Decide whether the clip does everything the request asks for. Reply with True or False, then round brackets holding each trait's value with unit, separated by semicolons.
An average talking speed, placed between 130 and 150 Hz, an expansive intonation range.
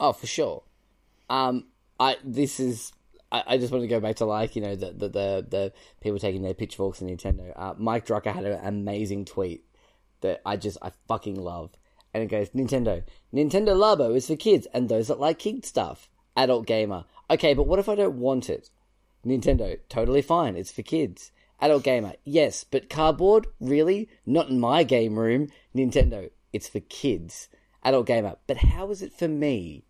False (190 wpm; 120 Hz; 6.0 semitones)